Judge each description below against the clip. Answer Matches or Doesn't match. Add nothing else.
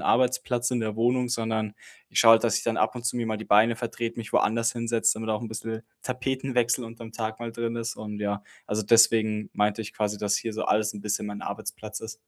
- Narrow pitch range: Matches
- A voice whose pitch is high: Doesn't match